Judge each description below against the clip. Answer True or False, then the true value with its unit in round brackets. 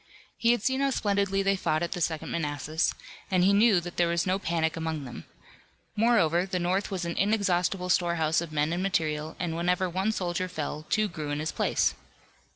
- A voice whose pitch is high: False (175 Hz)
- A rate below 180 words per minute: False (200 wpm)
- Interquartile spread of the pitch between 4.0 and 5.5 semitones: False (3.4 semitones)